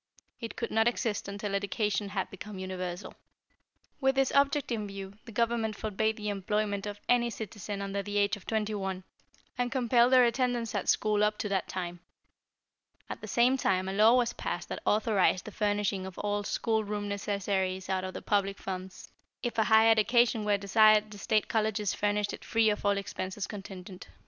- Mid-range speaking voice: No, high, 210 Hz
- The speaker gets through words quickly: No, average, 190 wpm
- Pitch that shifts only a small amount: Yes, narrow, 2.1 semitones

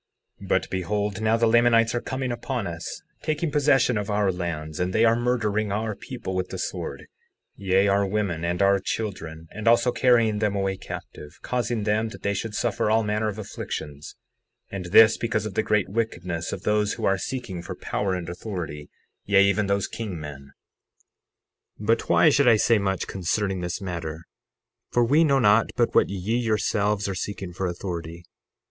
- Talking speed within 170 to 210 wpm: Yes, average, 185 wpm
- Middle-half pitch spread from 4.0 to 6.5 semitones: No, average, 3.6 semitones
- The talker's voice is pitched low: Yes, low, 105 Hz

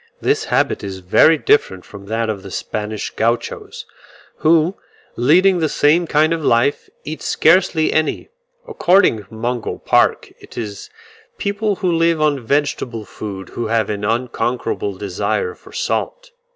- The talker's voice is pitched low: Yes, low, 130 Hz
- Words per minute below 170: Yes, average, 145 wpm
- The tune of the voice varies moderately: No, wide, 7.4 semitones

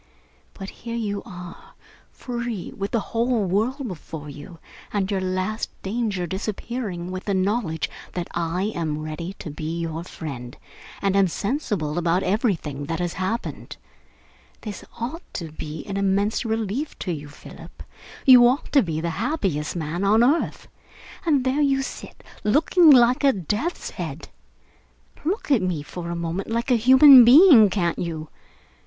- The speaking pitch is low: No, high, 195 Hz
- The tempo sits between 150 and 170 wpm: Yes, average, 155 wpm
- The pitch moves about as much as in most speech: No, wide, 5.9 semitones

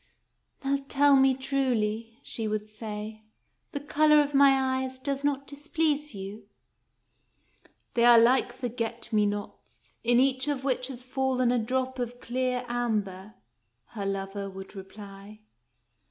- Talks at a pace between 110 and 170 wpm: Yes, average, 155 wpm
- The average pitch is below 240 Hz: No, high, 245 Hz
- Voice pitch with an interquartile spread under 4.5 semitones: Yes, average, 3.9 semitones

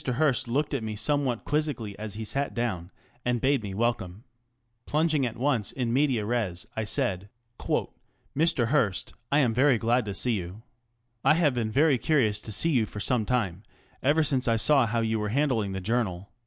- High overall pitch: No, low, 120 Hz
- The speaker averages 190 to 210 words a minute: Yes, average, 195 wpm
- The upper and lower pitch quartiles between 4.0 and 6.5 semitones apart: Yes, average, 4.6 semitones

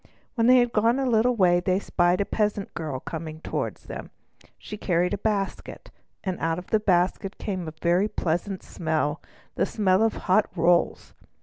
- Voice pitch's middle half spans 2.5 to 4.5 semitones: Yes, average, 3.6 semitones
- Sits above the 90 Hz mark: Yes, medium, 185 Hz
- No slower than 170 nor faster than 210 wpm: Yes, average, 175 wpm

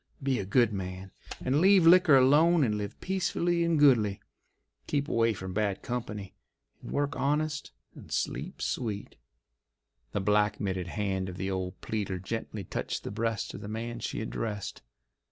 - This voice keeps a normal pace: Yes, average, 160 wpm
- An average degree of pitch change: No, wide, 6.2 semitones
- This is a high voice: No, low, 110 Hz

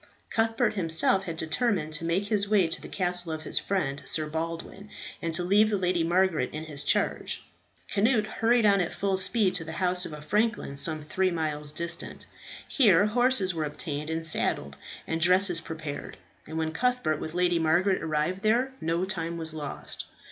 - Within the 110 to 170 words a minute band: No, average, 185 wpm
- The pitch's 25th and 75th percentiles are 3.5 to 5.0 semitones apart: Yes, average, 3.9 semitones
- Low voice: No, medium, 175 Hz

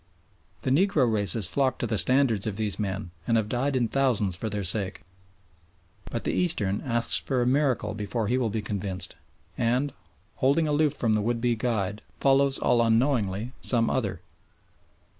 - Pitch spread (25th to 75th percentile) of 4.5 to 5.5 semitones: No, average, 4.1 semitones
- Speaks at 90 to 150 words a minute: No, average, 170 wpm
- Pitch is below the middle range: Yes, low, 115 Hz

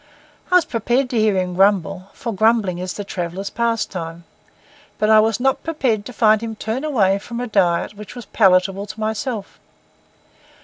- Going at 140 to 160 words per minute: No, average, 175 wpm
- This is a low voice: No, high, 215 Hz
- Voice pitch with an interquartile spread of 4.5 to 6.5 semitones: No, average, 3.3 semitones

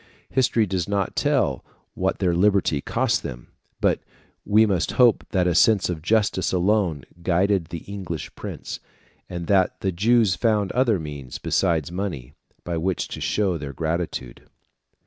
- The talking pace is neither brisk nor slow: Yes, average, 150 wpm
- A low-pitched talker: Yes, very low, 90 Hz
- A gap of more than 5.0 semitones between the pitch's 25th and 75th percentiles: No, average, 3.6 semitones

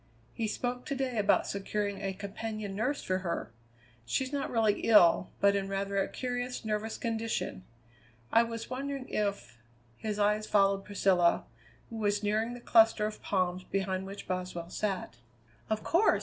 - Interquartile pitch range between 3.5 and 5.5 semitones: No, average, 2.8 semitones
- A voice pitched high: Yes, high, 210 Hz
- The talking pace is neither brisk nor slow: Yes, average, 165 wpm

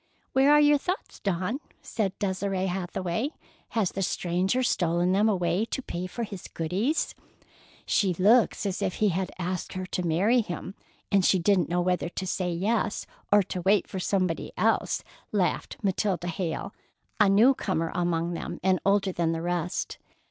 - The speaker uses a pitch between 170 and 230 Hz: Yes, high, 190 Hz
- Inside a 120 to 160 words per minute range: No, average, 170 wpm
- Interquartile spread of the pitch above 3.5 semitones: No, average, 2.8 semitones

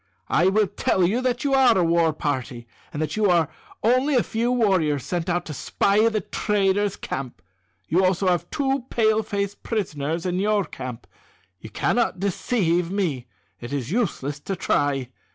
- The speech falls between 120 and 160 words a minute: No, average, 170 wpm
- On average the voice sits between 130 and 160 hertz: No, high, 190 Hz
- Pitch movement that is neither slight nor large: No, wide, 5.7 semitones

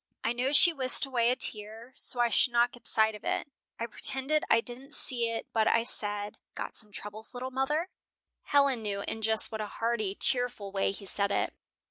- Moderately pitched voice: No, high, 230 Hz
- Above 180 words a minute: Yes, fast, 205 wpm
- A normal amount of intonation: Yes, average, 3.1 semitones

